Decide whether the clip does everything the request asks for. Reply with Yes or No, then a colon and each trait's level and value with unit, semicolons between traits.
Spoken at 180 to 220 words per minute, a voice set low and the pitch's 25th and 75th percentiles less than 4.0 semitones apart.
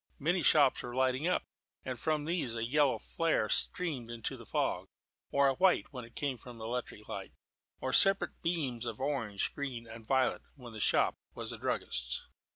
No: average, 185 wpm; low, 130 Hz; average, 4.3 semitones